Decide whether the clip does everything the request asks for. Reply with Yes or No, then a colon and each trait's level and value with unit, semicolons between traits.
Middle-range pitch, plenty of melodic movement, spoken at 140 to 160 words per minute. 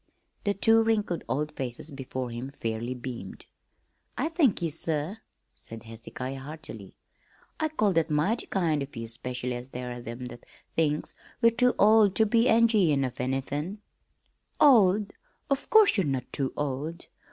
Yes: medium, 150 Hz; wide, 8.7 semitones; average, 155 wpm